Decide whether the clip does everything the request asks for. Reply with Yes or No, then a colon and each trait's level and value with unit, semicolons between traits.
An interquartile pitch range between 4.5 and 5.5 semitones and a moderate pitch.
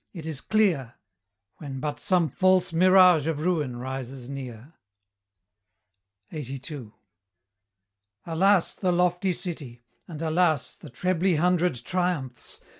Yes: average, 5.0 semitones; medium, 160 Hz